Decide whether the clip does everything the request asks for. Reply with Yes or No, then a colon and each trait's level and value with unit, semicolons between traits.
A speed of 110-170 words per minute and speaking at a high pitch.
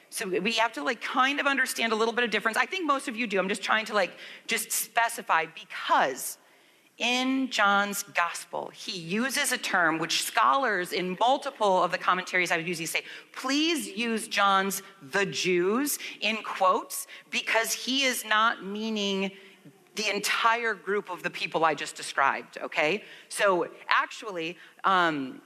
Yes: average, 165 wpm; high, 215 Hz